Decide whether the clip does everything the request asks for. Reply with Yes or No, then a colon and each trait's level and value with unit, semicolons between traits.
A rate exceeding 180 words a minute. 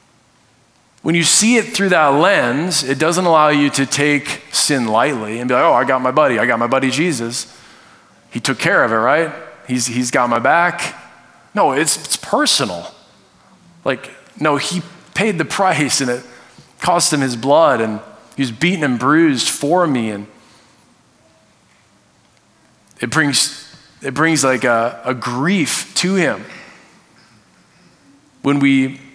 No: average, 155 wpm